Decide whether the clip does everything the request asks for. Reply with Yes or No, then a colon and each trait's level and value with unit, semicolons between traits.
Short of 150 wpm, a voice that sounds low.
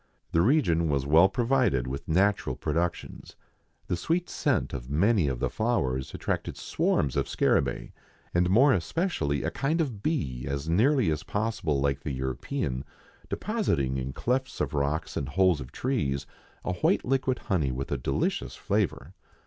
No: average, 155 wpm; very low, 85 Hz